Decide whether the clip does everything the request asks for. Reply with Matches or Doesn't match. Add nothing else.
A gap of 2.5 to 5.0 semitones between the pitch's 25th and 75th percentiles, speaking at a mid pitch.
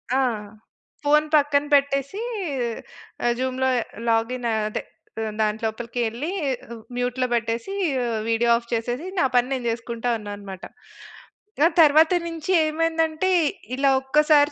Doesn't match